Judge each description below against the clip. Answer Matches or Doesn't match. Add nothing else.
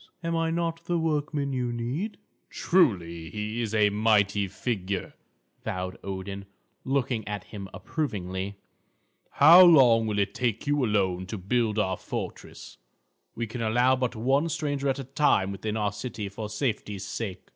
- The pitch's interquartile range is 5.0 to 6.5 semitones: Matches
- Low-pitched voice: Matches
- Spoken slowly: Doesn't match